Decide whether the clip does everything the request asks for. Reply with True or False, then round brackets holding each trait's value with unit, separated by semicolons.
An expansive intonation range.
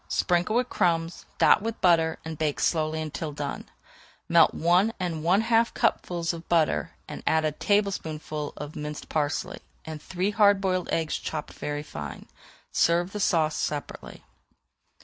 False (3.2 semitones)